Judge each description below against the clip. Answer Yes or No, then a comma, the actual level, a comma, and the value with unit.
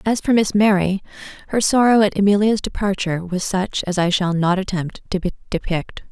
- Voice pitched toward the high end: Yes, high, 195 Hz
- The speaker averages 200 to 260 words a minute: No, average, 175 wpm